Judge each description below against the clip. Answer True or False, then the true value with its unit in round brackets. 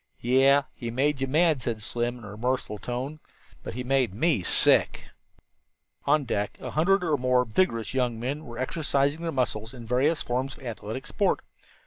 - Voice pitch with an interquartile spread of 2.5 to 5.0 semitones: True (3.5 semitones)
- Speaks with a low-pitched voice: True (130 Hz)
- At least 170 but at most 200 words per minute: True (175 wpm)